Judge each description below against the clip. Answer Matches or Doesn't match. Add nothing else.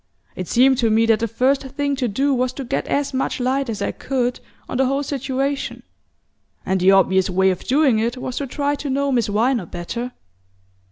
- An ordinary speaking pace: Doesn't match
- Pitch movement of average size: Matches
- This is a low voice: Doesn't match